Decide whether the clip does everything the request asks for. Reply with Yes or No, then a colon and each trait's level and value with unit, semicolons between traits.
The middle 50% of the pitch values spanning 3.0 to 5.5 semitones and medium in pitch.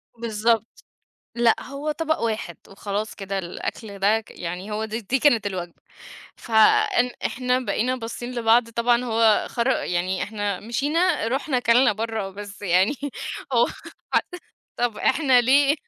No: average, 3.5 semitones; high, 225 Hz